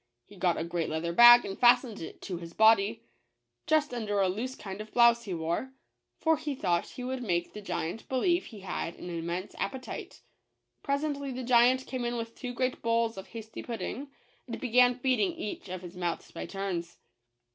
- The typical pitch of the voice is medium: No, high, 225 Hz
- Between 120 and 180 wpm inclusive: No, average, 195 wpm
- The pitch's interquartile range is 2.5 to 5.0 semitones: No, wide, 5.6 semitones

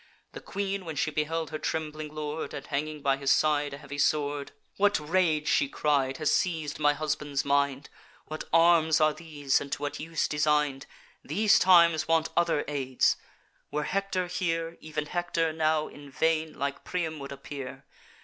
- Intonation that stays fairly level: Yes, narrow, 2.2 semitones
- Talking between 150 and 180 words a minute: Yes, average, 170 wpm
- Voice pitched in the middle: Yes, medium, 155 Hz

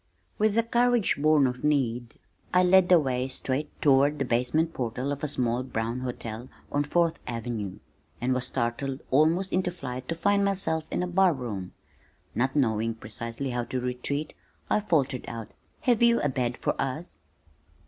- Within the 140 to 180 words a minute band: Yes, average, 170 wpm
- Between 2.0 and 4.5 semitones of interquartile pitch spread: No, wide, 5.4 semitones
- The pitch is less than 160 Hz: Yes, low, 135 Hz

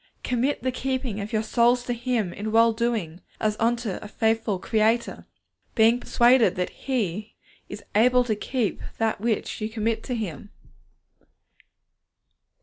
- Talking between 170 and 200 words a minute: No, average, 145 wpm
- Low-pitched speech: No, high, 225 Hz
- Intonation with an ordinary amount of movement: No, narrow, 2.2 semitones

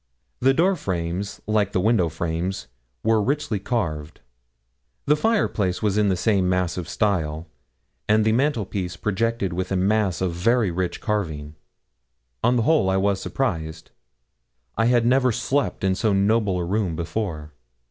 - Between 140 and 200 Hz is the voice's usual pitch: No, low, 100 Hz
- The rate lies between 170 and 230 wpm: No, average, 150 wpm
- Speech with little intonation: No, average, 4.2 semitones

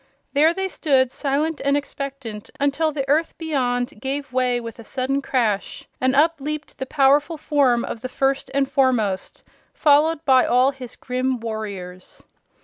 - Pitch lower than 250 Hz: No, very high, 270 Hz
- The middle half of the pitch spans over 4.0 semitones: No, average, 2.8 semitones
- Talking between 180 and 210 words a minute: No, average, 155 wpm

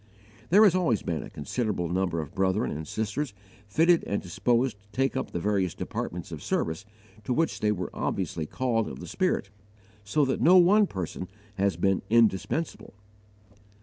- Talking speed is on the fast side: No, average, 170 wpm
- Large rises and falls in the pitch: Yes, wide, 6.4 semitones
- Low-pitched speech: Yes, low, 105 Hz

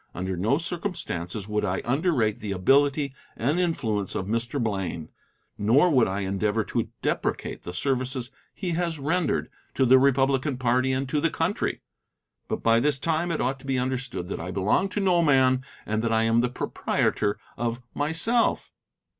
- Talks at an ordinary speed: Yes, average, 170 wpm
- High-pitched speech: No, low, 130 Hz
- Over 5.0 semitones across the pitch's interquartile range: Yes, wide, 5.5 semitones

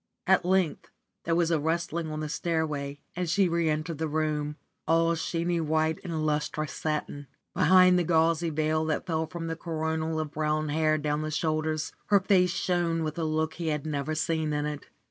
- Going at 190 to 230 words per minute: Yes, average, 195 wpm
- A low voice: No, medium, 160 Hz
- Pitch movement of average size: No, narrow, 1.5 semitones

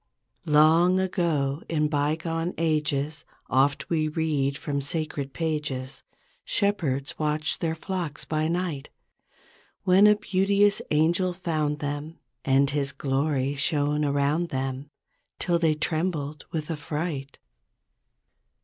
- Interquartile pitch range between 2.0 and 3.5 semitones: Yes, average, 2.8 semitones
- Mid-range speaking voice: Yes, medium, 155 Hz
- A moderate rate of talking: No, slow, 110 wpm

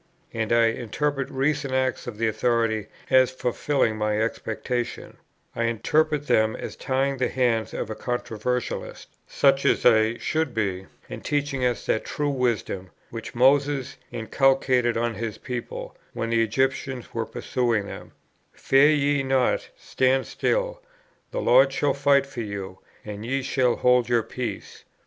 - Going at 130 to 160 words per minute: Yes, average, 150 wpm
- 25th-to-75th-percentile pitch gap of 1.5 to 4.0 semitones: Yes, average, 3.1 semitones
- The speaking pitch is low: Yes, low, 125 Hz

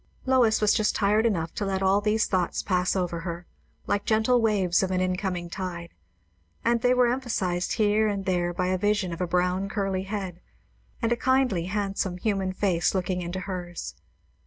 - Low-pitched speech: No, high, 190 Hz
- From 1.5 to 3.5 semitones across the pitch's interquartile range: Yes, average, 2.8 semitones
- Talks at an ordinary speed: Yes, average, 185 wpm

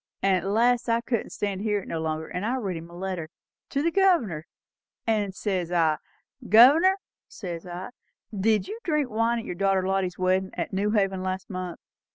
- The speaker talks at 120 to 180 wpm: No, average, 190 wpm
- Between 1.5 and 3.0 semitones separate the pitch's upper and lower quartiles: No, average, 4.0 semitones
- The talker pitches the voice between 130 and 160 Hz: No, high, 195 Hz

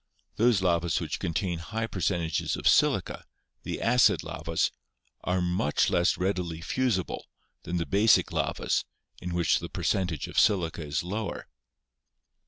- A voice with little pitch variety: No, average, 3.0 semitones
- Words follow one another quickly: No, slow, 135 wpm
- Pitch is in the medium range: No, very low, 90 Hz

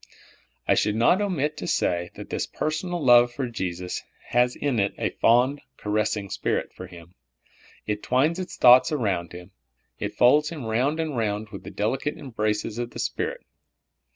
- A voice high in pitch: No, low, 120 Hz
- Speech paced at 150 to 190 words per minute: Yes, average, 170 wpm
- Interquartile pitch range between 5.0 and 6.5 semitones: Yes, wide, 5.5 semitones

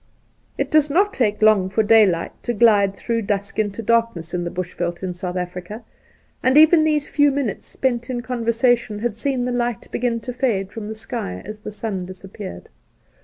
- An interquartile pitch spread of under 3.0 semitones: No, average, 4.0 semitones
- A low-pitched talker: No, high, 220 Hz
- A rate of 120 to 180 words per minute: No, average, 190 wpm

